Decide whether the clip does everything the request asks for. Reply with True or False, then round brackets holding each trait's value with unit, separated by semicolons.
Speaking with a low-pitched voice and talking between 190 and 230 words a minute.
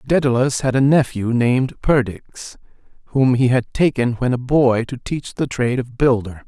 False (125 Hz; 175 wpm)